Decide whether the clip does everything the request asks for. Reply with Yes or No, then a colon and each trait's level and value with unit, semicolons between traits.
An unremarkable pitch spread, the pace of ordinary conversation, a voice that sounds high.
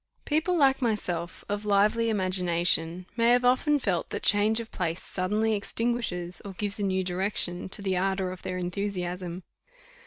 Yes: average, 3.6 semitones; average, 160 wpm; high, 195 Hz